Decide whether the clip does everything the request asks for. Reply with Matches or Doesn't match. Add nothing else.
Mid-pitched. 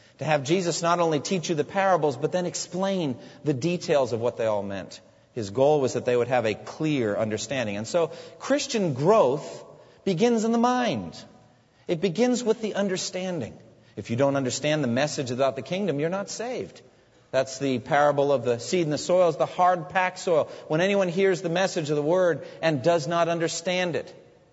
Matches